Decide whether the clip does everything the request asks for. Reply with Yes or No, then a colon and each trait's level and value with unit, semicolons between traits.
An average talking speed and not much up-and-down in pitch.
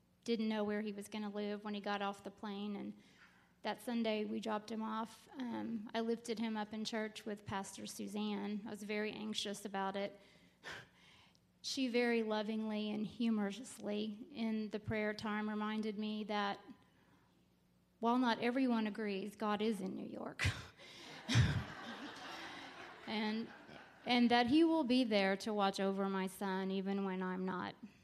Yes: average, 160 wpm; narrow, 1.7 semitones